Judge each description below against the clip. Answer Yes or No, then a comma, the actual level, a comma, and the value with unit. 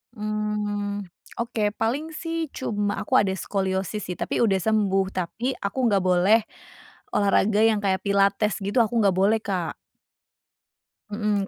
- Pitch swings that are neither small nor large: No, narrow, 2.1 semitones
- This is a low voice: No, high, 205 Hz